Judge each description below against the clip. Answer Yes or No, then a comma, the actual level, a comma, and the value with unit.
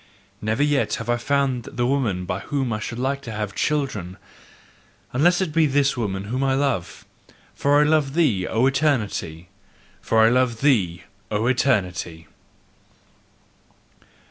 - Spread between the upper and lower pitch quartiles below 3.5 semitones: No, average, 5.1 semitones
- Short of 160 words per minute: Yes, average, 145 wpm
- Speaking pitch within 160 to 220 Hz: No, low, 125 Hz